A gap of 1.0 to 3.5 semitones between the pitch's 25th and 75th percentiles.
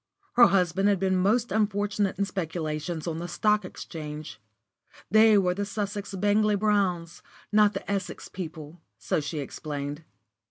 No: average, 4.1 semitones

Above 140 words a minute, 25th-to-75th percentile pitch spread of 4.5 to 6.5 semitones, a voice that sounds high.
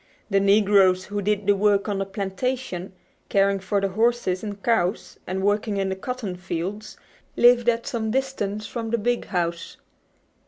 No: average, 165 wpm; average, 2.9 semitones; high, 205 Hz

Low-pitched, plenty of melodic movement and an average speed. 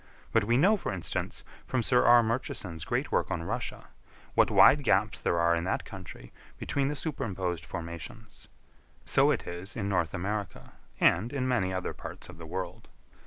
Yes: very low, 95 Hz; wide, 5.8 semitones; average, 175 wpm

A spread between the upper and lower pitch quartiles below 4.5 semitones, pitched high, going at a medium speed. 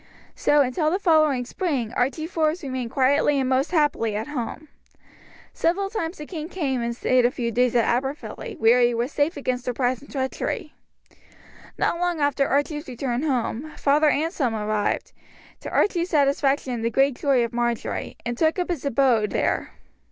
Yes: average, 4.1 semitones; very high, 275 Hz; average, 175 wpm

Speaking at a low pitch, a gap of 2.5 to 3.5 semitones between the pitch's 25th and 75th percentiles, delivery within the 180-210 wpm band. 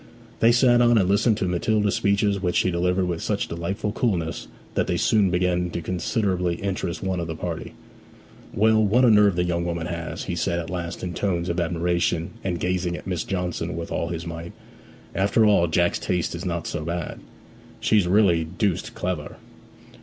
Yes: very low, 90 Hz; average, 2.8 semitones; average, 190 wpm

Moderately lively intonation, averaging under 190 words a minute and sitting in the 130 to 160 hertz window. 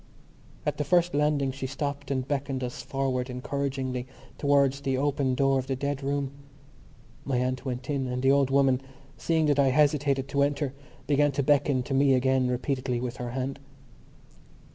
No: narrow, 1.6 semitones; average, 175 wpm; low, 135 Hz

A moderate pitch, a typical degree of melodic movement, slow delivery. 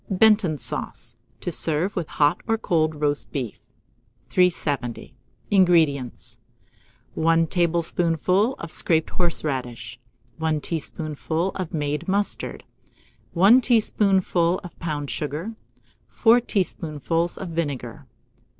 Yes: medium, 165 Hz; average, 3.7 semitones; slow, 100 wpm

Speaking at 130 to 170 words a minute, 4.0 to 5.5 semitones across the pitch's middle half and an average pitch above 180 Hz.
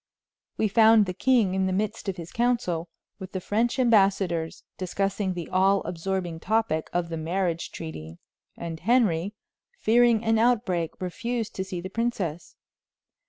Yes: average, 150 wpm; average, 4.5 semitones; high, 190 Hz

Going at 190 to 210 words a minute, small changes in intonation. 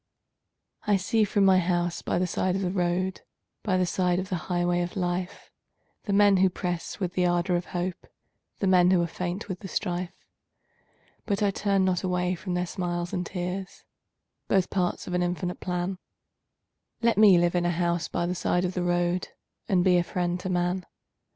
Yes: average, 195 wpm; narrow, 1.2 semitones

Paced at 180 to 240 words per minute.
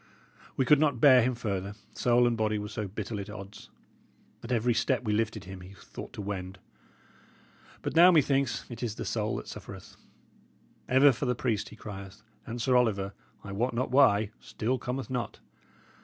Yes: average, 185 wpm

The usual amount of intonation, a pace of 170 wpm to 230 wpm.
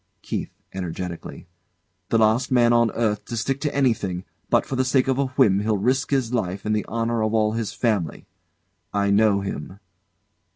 Yes: average, 3.7 semitones; average, 180 wpm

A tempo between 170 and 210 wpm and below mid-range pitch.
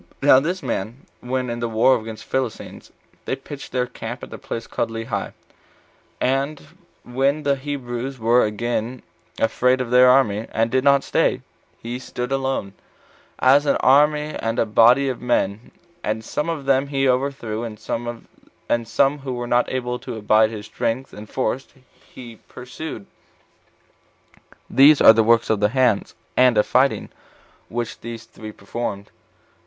No: average, 160 wpm; low, 125 Hz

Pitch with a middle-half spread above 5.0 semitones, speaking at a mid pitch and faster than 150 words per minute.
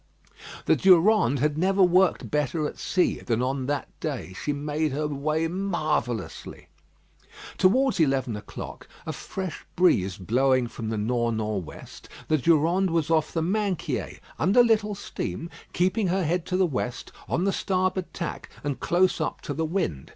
Yes: wide, 5.5 semitones; medium, 160 Hz; average, 160 wpm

